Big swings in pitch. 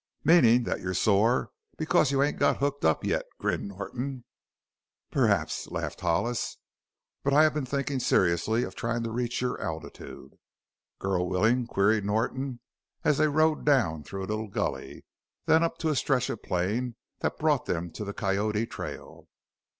Yes: wide, 5.8 semitones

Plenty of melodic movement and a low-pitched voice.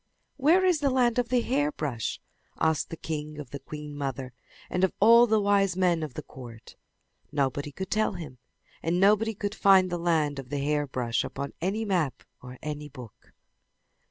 No: wide, 6.7 semitones; medium, 165 Hz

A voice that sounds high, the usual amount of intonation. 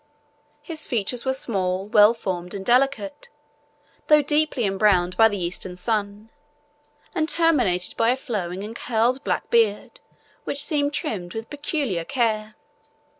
No: high, 225 Hz; wide, 5.9 semitones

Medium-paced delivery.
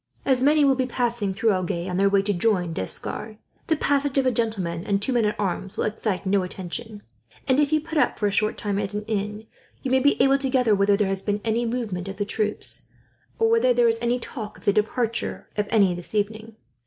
No: fast, 240 wpm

